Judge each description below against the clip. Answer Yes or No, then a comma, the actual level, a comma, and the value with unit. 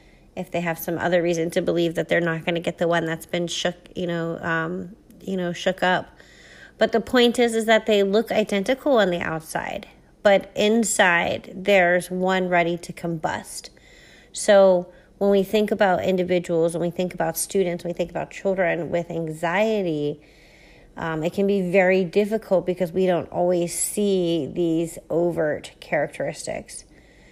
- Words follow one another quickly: No, average, 170 wpm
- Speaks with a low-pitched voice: No, medium, 180 Hz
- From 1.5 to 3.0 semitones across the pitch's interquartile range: Yes, narrow, 2.6 semitones